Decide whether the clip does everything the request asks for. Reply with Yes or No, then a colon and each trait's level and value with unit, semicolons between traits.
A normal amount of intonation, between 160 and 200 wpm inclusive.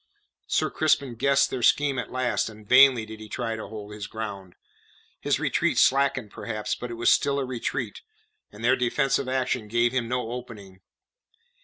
Yes: average, 3.1 semitones; average, 175 wpm